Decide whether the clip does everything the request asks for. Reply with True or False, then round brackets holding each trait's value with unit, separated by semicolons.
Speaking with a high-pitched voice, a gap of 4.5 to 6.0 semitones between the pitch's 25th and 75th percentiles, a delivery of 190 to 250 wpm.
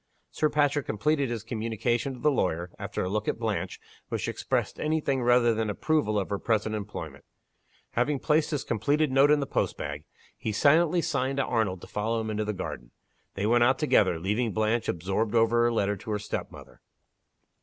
False (115 Hz; 4.8 semitones; 195 wpm)